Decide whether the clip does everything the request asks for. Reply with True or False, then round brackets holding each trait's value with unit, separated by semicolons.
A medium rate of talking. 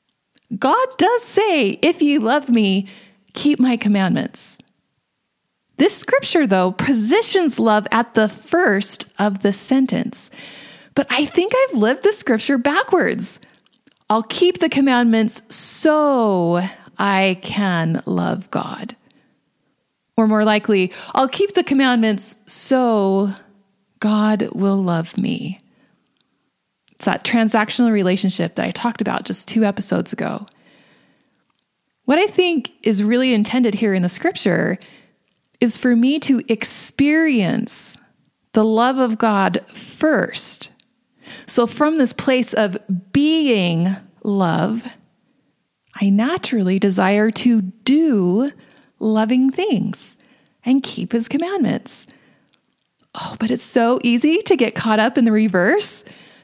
False (120 wpm)